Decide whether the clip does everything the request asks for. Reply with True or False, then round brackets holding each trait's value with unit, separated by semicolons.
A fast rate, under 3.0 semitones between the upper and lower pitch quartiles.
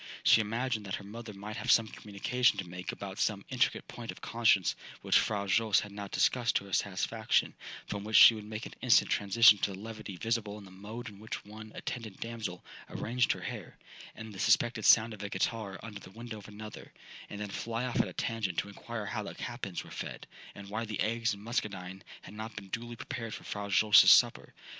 True (220 wpm; 2.4 semitones)